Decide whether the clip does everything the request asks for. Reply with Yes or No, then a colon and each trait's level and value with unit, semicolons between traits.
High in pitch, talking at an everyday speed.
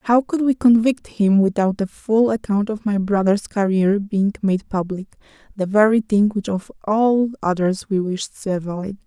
Yes: high, 205 Hz; average, 170 wpm